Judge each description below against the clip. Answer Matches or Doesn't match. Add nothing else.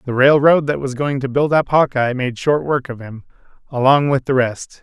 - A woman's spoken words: Doesn't match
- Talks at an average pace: Doesn't match